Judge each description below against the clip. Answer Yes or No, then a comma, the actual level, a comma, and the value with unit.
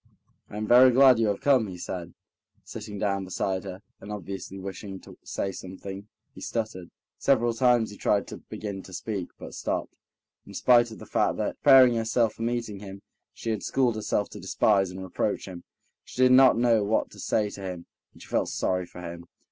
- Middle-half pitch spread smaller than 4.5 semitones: Yes, average, 3.5 semitones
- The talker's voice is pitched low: Yes, low, 105 Hz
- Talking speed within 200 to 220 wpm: Yes, fast, 205 wpm